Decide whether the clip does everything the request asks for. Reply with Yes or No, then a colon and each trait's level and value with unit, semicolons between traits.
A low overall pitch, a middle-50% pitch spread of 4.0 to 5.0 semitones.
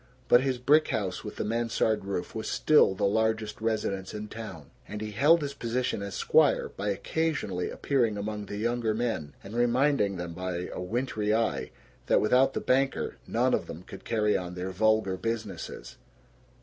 No: low, 110 Hz; average, 3.6 semitones